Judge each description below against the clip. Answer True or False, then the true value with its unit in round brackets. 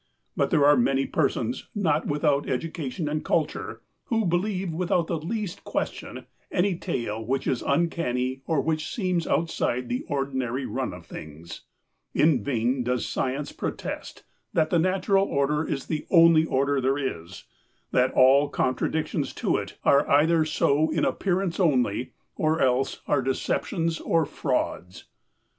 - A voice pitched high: False (145 Hz)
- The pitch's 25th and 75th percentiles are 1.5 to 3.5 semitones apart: False (4.2 semitones)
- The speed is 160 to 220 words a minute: False (145 wpm)